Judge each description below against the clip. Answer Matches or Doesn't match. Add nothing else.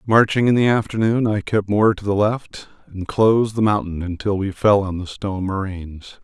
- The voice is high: Doesn't match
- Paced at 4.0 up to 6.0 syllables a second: Matches